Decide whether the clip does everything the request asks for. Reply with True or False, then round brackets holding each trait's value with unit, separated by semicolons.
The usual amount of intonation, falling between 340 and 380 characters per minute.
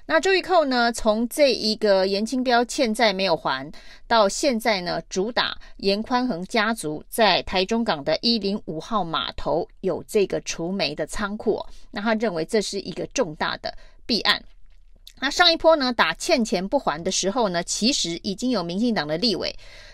False (4.4 semitones; 255 characters per minute)